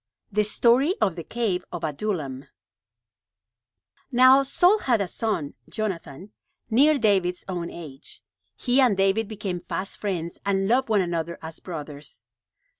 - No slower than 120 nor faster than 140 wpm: Yes, slow, 135 wpm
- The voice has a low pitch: No, high, 195 Hz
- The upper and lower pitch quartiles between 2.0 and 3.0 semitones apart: No, average, 5.2 semitones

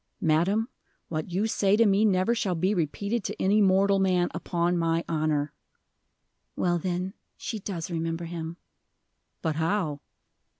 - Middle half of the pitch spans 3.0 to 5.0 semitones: Yes, average, 3.3 semitones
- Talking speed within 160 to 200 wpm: No, average, 140 wpm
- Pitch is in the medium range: Yes, medium, 180 Hz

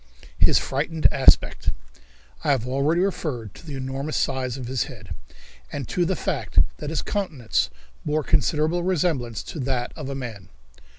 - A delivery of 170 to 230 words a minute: No, average, 160 wpm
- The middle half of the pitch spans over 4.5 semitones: No, average, 3.8 semitones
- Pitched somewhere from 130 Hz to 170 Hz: Yes, medium, 140 Hz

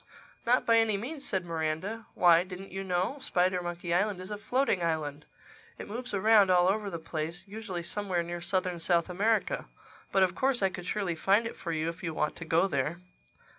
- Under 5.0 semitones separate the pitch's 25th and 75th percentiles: Yes, average, 3.4 semitones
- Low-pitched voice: No, medium, 185 Hz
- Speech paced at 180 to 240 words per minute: Yes, average, 190 wpm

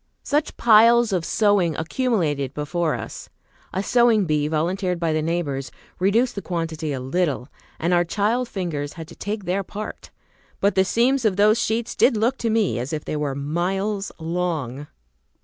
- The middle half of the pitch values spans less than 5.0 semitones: No, wide, 5.4 semitones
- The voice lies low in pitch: No, medium, 180 Hz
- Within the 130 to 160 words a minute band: No, average, 170 wpm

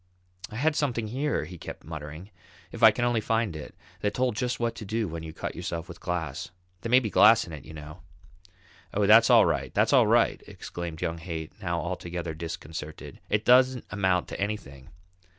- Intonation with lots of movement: Yes, wide, 5.9 semitones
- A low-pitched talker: Yes, very low, 95 Hz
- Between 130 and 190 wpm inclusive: No, average, 200 wpm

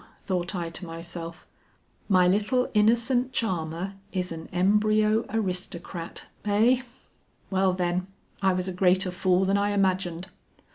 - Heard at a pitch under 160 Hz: No, medium, 185 Hz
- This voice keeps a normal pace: No, slow, 130 wpm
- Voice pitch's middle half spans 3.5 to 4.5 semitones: No, average, 2.8 semitones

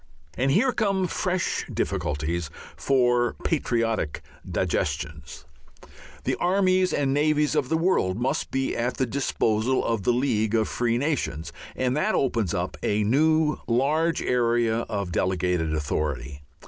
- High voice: No, low, 120 Hz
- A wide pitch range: Yes, wide, 6.5 semitones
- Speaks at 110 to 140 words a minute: Yes, slow, 135 wpm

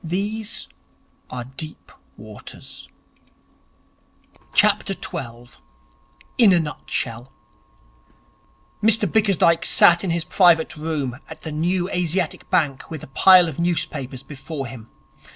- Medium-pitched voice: Yes, medium, 160 Hz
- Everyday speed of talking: No, slow, 105 wpm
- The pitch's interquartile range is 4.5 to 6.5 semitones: Yes, average, 5.0 semitones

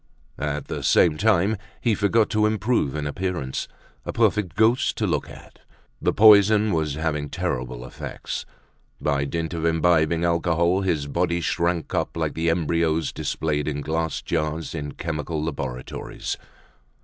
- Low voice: Yes, very low, 80 Hz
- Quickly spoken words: No, average, 145 wpm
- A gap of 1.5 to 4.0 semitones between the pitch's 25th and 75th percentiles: Yes, average, 3.4 semitones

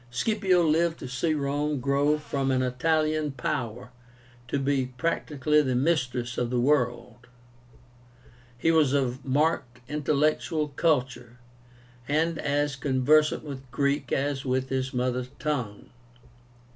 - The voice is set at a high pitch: No, medium, 140 Hz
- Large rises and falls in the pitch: No, average, 3.0 semitones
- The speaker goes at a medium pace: No, slow, 120 wpm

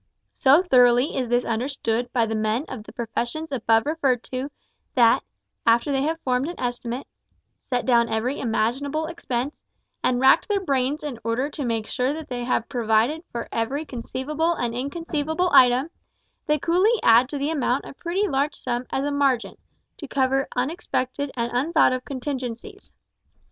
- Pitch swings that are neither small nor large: Yes, average, 3.6 semitones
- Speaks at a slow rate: No, average, 165 wpm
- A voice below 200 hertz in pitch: No, very high, 260 Hz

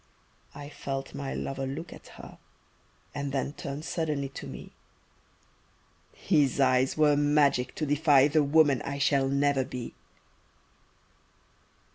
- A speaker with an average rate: No, slow, 125 wpm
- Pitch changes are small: Yes, narrow, 1.5 semitones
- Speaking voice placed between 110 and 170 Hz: Yes, medium, 140 Hz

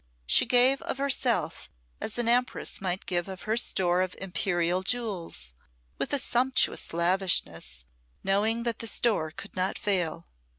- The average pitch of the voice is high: Yes, high, 195 Hz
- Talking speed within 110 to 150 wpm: Yes, average, 140 wpm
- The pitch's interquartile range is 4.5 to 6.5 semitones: Yes, average, 5.2 semitones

